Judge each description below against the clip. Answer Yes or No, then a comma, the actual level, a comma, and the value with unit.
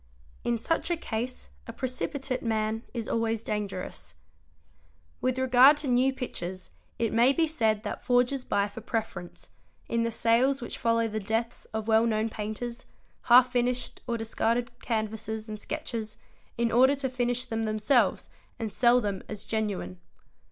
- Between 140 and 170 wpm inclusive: Yes, average, 155 wpm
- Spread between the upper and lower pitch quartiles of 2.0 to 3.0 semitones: Yes, narrow, 2.4 semitones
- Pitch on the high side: Yes, high, 230 Hz